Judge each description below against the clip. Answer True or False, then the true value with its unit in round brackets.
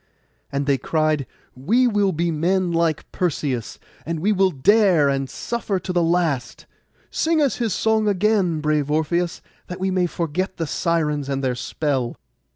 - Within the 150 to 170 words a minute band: True (160 wpm)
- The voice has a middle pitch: True (170 Hz)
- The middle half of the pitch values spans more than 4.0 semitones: True (4.4 semitones)